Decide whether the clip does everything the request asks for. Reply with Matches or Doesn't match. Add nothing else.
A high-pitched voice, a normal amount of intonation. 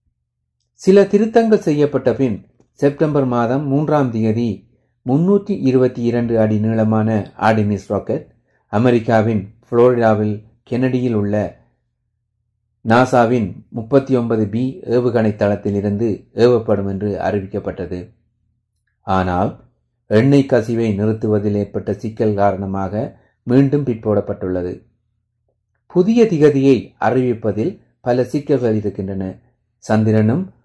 Doesn't match